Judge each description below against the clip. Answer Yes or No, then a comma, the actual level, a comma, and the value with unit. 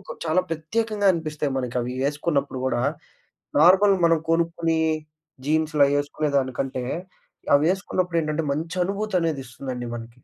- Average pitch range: Yes, average, 3.5 semitones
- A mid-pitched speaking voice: Yes, medium, 155 Hz